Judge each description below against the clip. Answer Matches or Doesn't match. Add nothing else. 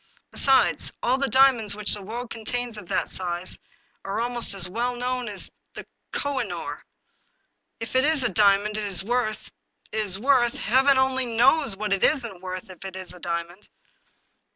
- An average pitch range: Matches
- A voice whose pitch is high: Matches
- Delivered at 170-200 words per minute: Matches